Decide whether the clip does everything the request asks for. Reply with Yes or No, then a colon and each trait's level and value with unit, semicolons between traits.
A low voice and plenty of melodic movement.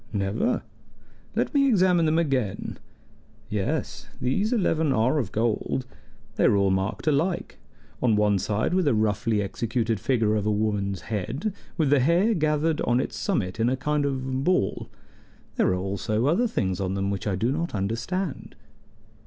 Yes: low, 120 Hz; wide, 7.2 semitones